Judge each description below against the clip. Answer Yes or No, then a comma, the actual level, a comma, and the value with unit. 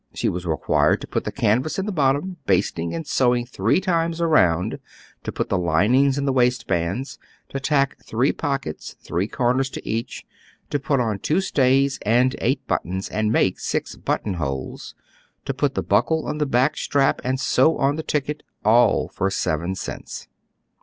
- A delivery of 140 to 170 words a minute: No, average, 180 wpm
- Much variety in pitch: Yes, wide, 6.5 semitones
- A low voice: Yes, low, 130 Hz